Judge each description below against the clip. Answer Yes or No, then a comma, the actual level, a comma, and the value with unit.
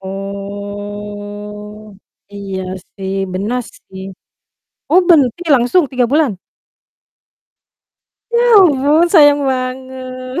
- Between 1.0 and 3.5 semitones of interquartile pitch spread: No, average, 5.1 semitones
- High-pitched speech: Yes, high, 240 Hz